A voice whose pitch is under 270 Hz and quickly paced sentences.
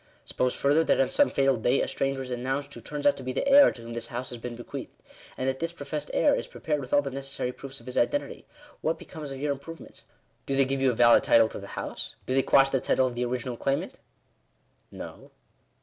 Yes: low, 135 Hz; fast, 250 wpm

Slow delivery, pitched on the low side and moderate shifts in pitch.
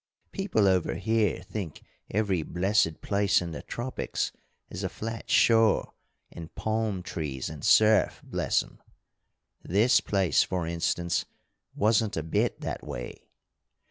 Yes: slow, 130 wpm; low, 100 Hz; average, 4.4 semitones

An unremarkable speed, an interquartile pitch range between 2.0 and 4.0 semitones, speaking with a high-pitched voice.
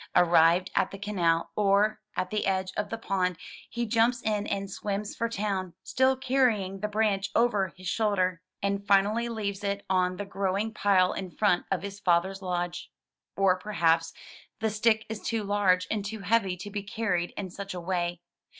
Yes: average, 180 wpm; narrow, 2.5 semitones; high, 200 Hz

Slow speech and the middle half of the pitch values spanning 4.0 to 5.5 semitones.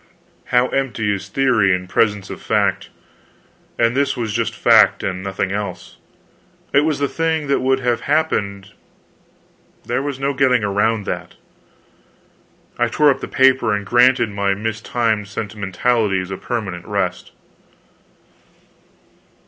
Yes: slow, 130 wpm; average, 4.7 semitones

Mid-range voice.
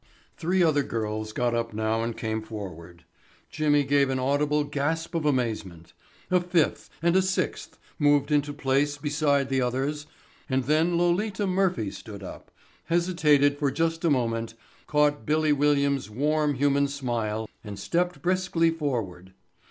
Yes: medium, 145 Hz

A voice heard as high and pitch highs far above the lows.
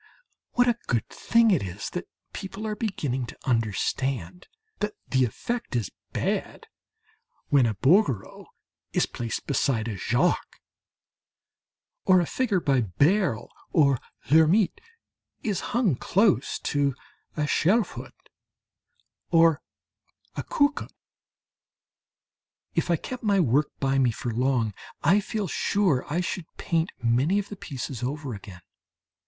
No: medium, 150 Hz; wide, 7.9 semitones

